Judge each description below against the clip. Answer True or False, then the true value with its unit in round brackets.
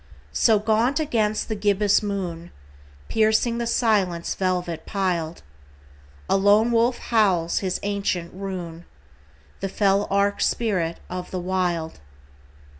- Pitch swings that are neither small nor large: True (3.4 semitones)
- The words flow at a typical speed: False (115 wpm)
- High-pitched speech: True (195 Hz)